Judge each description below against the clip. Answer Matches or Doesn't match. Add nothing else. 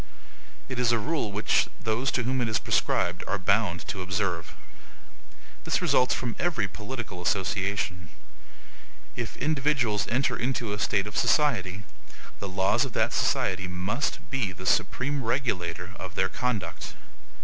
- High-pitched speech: Doesn't match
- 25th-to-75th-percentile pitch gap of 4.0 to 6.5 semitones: Matches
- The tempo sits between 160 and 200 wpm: Doesn't match